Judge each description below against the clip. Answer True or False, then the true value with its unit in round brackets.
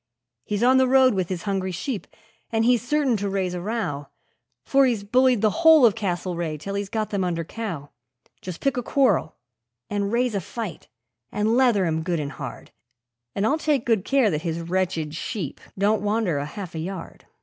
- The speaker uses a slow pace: False (200 wpm)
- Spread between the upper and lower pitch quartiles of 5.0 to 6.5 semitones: True (5.4 semitones)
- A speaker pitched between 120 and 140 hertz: False (200 Hz)